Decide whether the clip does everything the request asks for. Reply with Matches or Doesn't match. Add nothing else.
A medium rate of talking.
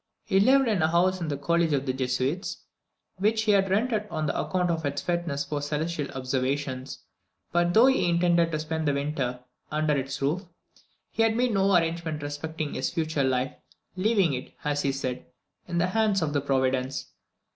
Matches